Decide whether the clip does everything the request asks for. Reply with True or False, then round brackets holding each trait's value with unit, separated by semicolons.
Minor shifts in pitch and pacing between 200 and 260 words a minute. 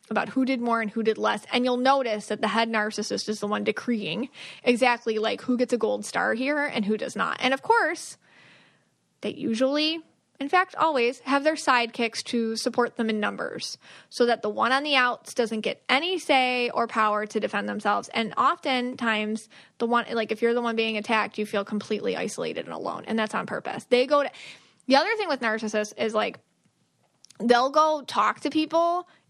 False (3.5 semitones; 205 wpm)